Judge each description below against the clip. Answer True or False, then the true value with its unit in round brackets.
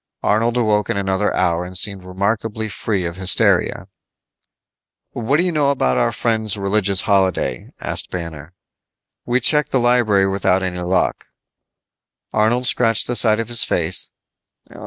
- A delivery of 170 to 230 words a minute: False (145 wpm)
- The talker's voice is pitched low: True (105 Hz)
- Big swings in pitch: False (3.8 semitones)